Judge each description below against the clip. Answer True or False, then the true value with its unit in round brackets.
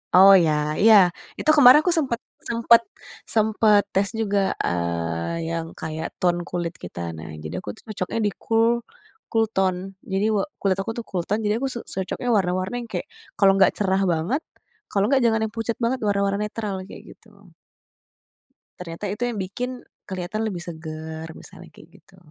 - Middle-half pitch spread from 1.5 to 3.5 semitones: False (4.3 semitones)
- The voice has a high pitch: True (195 Hz)